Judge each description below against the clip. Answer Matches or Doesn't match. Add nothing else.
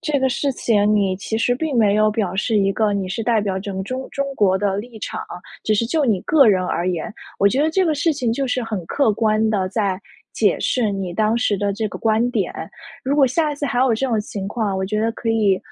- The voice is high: Matches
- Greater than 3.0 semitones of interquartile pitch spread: Matches